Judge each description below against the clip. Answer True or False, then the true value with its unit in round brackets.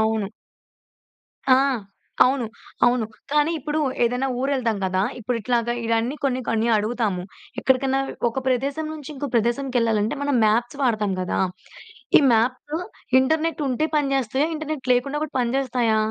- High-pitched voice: True (250 Hz)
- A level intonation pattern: False (3.4 semitones)